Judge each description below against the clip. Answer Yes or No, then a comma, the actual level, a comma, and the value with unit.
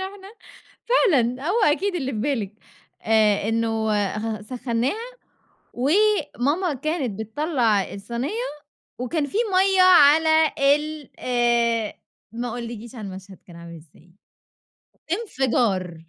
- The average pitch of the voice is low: No, high, 245 Hz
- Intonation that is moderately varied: No, wide, 6.6 semitones